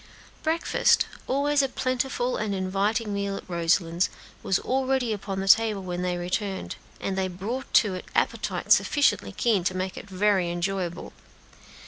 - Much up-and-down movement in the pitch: No, average, 4.2 semitones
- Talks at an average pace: Yes, average, 150 wpm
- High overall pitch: Yes, high, 195 Hz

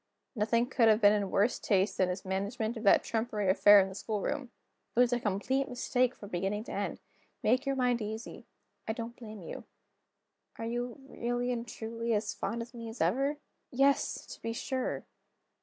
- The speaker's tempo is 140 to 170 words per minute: No, average, 190 wpm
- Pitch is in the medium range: No, high, 230 Hz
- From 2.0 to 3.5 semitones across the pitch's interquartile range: Yes, average, 2.9 semitones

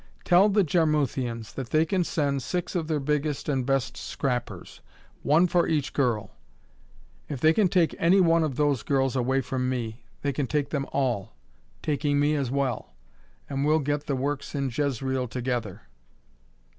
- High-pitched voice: No, medium, 140 Hz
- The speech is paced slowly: No, average, 170 wpm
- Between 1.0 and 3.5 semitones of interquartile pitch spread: Yes, average, 3.0 semitones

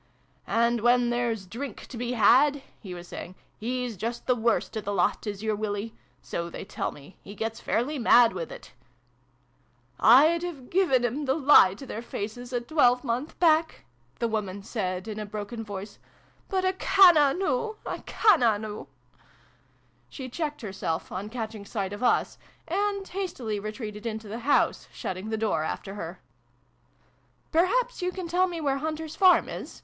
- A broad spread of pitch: Yes, wide, 6.3 semitones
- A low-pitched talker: No, high, 235 Hz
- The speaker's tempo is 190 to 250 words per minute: No, average, 180 wpm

